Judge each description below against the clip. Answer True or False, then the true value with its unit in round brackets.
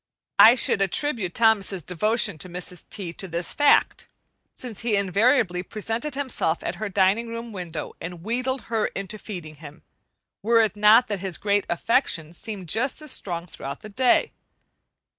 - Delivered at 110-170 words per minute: True (160 wpm)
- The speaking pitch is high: True (205 Hz)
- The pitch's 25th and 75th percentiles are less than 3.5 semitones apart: False (4.5 semitones)